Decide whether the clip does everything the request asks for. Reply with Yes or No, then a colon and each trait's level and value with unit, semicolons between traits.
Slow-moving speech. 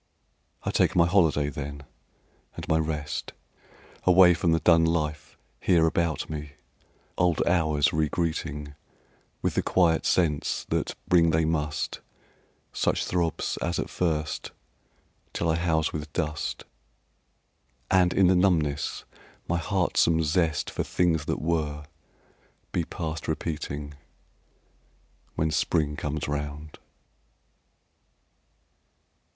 Yes: slow, 115 wpm